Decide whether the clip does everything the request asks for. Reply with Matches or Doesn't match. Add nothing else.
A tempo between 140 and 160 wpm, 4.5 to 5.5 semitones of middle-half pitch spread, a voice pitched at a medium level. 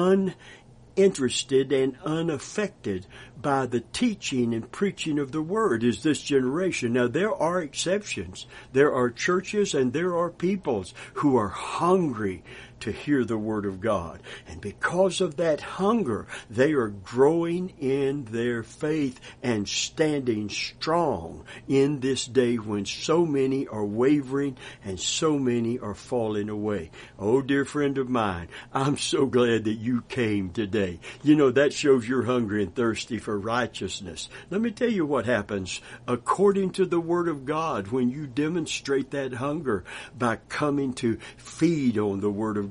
Doesn't match